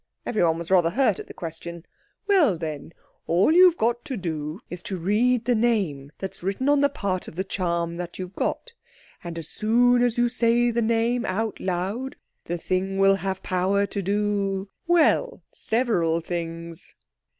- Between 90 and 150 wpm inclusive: No, average, 165 wpm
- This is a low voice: No, high, 195 Hz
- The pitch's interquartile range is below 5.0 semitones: No, wide, 5.5 semitones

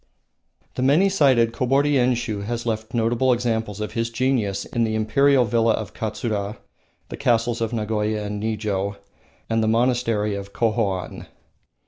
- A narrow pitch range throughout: Yes, narrow, 2.3 semitones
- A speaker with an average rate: Yes, average, 145 wpm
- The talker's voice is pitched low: Yes, low, 115 Hz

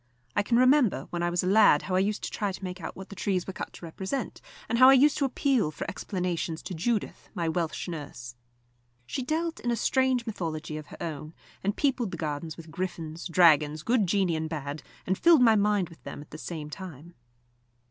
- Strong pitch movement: Yes, wide, 5.9 semitones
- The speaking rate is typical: No, fast, 220 wpm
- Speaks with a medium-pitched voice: Yes, medium, 180 Hz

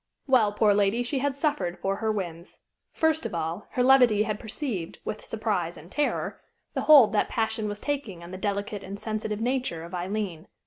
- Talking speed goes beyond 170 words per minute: Yes, average, 190 wpm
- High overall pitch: Yes, high, 210 Hz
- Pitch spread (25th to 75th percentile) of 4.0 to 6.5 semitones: Yes, average, 4.5 semitones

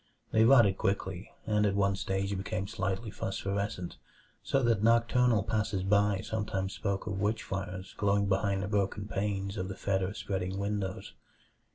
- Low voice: Yes, low, 100 Hz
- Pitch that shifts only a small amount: Yes, narrow, 1.5 semitones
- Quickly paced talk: No, average, 155 wpm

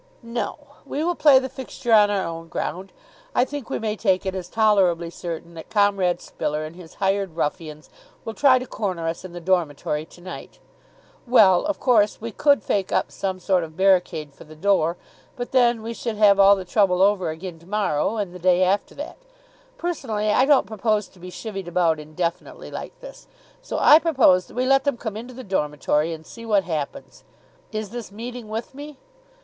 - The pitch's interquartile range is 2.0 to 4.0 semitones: No, average, 5.0 semitones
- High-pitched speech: Yes, high, 195 Hz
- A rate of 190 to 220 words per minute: Yes, average, 200 wpm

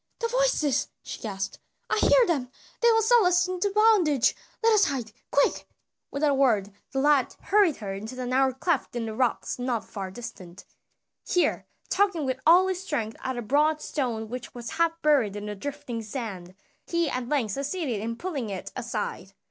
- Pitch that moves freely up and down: Yes, wide, 7.1 semitones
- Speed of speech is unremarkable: Yes, average, 185 wpm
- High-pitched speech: Yes, very high, 270 Hz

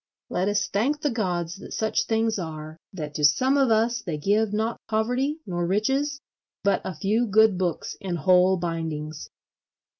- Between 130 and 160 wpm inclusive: No, average, 170 wpm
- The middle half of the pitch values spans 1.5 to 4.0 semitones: No, average, 4.5 semitones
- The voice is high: Yes, high, 200 Hz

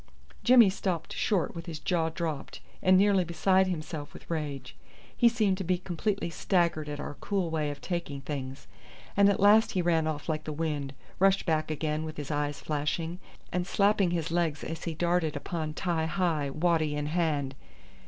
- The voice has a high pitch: No, medium, 165 Hz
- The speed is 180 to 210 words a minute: Yes, average, 185 wpm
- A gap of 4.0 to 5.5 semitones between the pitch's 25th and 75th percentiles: No, average, 3.2 semitones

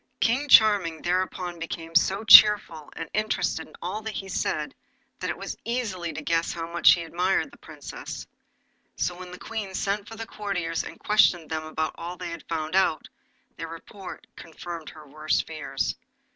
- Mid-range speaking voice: Yes, medium, 175 Hz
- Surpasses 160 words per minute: Yes, average, 170 wpm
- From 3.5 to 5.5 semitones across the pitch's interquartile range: Yes, average, 3.8 semitones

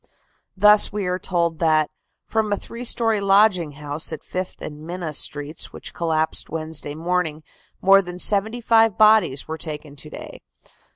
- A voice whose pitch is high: No, medium, 175 Hz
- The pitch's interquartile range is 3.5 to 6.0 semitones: Yes, average, 4.6 semitones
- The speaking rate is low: No, average, 160 wpm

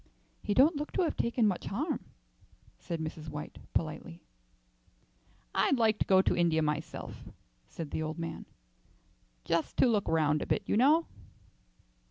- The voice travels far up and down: Yes, wide, 6.9 semitones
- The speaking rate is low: No, average, 155 wpm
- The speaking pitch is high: No, medium, 175 Hz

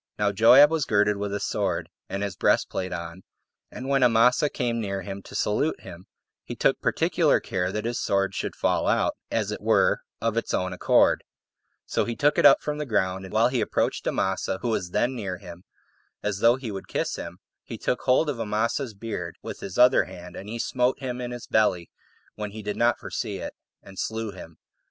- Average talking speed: No, fast, 210 wpm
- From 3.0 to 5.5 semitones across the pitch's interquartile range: Yes, average, 4.2 semitones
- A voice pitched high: No, low, 105 Hz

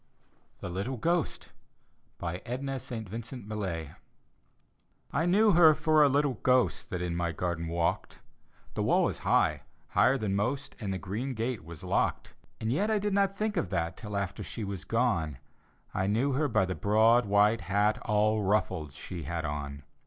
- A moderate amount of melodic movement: No, wide, 6.4 semitones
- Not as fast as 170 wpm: No, average, 180 wpm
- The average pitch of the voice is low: Yes, low, 105 Hz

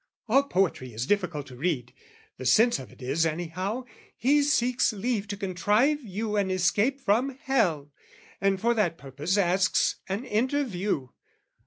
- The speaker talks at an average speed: Yes, average, 155 wpm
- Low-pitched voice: No, high, 195 Hz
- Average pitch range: No, wide, 6.1 semitones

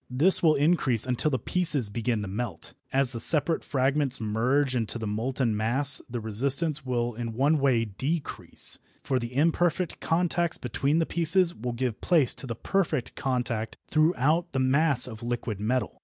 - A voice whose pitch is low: Yes, low, 130 Hz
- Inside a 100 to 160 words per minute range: No, average, 170 wpm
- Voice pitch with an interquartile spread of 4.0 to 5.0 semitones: Yes, average, 4.6 semitones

